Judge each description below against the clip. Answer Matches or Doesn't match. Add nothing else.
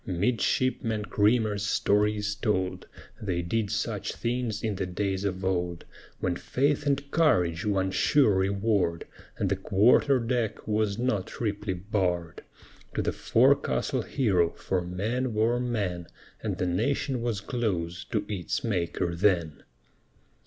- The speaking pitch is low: Matches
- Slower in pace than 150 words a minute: Matches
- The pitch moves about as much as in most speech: Matches